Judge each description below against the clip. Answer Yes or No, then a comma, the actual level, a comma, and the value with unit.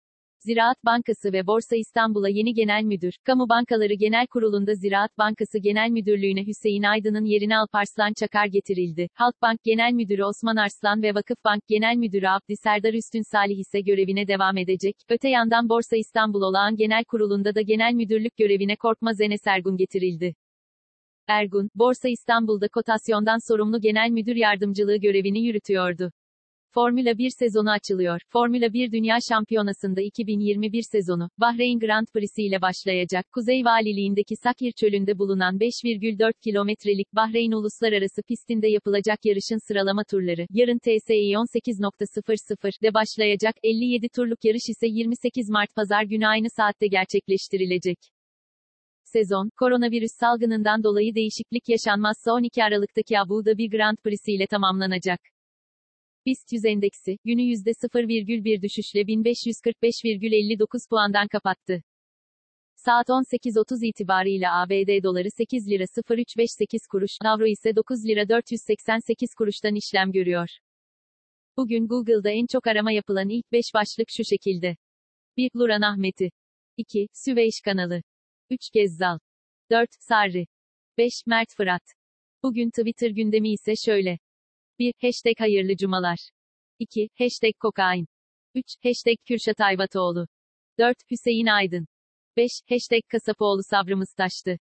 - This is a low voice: No, high, 215 Hz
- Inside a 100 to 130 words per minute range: Yes, average, 125 wpm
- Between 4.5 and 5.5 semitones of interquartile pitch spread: No, narrow, 2.4 semitones